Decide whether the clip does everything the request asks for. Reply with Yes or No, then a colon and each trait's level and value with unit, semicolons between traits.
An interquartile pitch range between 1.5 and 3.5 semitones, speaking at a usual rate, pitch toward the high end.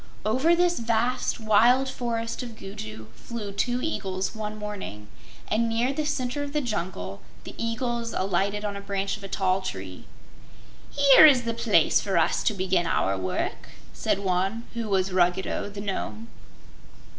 No: average, 4.0 semitones; average, 160 wpm; high, 210 Hz